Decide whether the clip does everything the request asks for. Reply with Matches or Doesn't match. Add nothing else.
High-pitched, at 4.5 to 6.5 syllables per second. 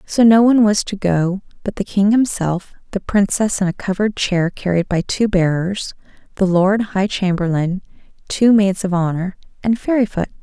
Matches